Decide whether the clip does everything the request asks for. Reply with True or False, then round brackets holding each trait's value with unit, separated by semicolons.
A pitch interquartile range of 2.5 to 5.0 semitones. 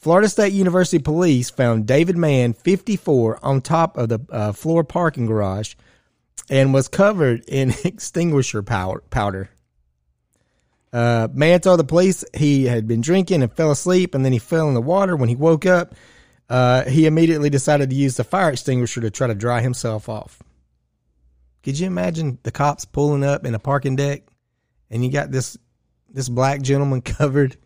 False (5.5 semitones)